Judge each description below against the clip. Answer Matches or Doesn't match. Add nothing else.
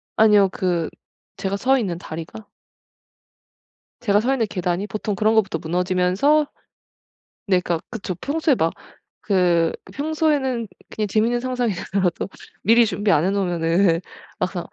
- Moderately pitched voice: Doesn't match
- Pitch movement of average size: Matches